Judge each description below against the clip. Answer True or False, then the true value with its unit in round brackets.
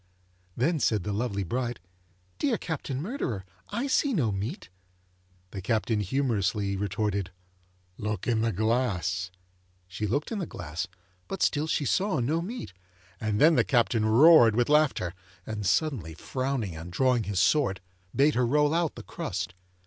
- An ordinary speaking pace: True (155 wpm)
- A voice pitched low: True (115 Hz)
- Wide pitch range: True (6.8 semitones)